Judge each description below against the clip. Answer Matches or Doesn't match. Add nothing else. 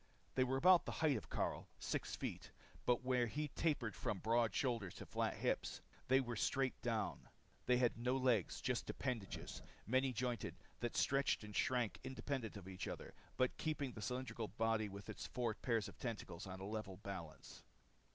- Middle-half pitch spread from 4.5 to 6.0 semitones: Doesn't match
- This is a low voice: Matches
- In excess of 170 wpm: Matches